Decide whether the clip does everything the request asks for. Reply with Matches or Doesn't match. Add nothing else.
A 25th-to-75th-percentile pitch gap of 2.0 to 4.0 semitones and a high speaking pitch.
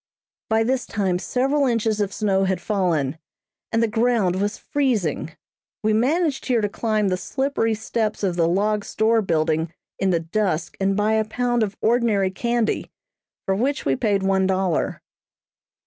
Matches